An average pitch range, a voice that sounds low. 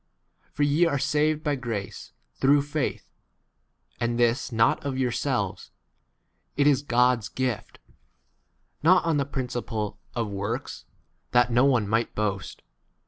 Yes: average, 3.9 semitones; low, 125 Hz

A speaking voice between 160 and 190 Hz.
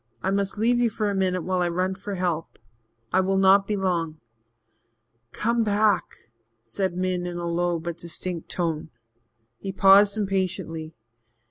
Yes: medium, 185 Hz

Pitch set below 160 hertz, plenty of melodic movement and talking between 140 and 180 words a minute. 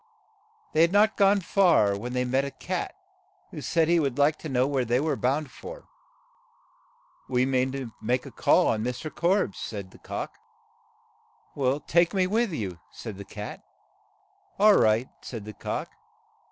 Yes: low, 135 Hz; wide, 6.1 semitones; average, 165 wpm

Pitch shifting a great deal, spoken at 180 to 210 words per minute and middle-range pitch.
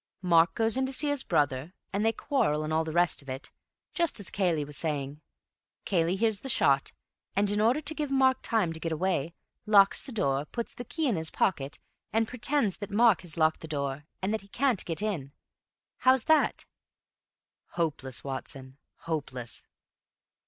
Yes: wide, 7.1 semitones; average, 185 wpm; medium, 180 Hz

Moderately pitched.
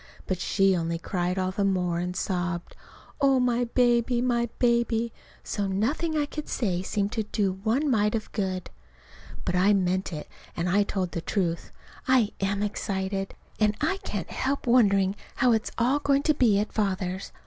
No: high, 205 Hz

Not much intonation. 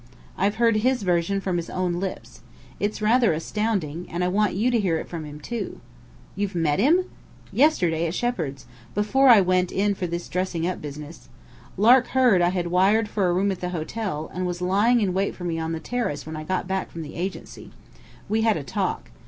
No: average, 3.9 semitones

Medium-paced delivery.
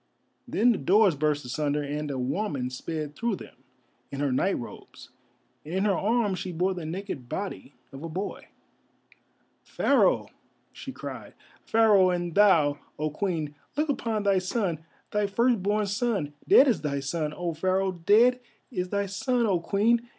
Yes: average, 155 wpm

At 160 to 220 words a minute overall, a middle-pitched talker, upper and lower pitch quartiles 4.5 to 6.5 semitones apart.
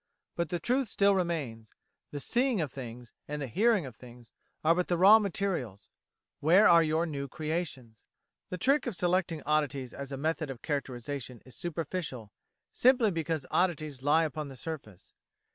Yes: average, 165 wpm; medium, 155 Hz; average, 5.1 semitones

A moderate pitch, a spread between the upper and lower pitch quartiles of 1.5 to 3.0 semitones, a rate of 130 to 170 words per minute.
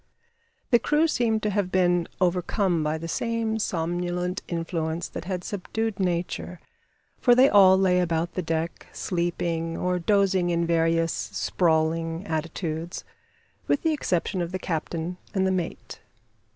Yes: medium, 175 Hz; narrow, 2.5 semitones; average, 140 wpm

